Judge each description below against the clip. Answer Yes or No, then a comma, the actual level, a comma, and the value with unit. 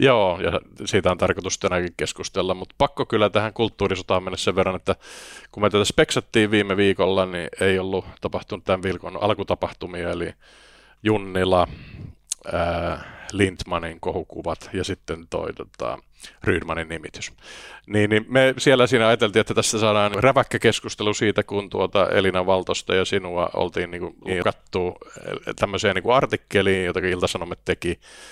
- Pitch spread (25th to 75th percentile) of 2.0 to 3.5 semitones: Yes, average, 2.9 semitones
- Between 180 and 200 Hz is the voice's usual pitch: No, low, 100 Hz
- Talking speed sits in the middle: Yes, average, 140 wpm